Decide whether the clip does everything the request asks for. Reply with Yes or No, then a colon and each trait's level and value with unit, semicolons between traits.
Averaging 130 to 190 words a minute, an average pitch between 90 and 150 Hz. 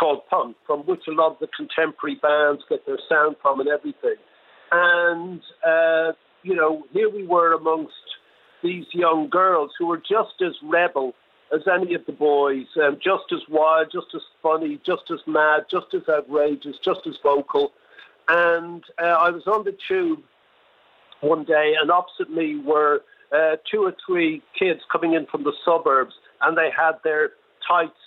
No: average, 175 wpm; medium, 170 Hz